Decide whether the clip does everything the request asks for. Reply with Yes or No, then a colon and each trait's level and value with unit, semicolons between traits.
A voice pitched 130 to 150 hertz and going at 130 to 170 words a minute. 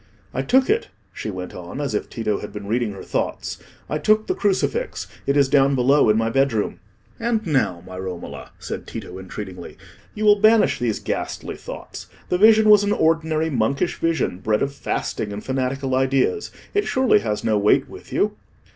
No: low, 135 Hz; average, 185 wpm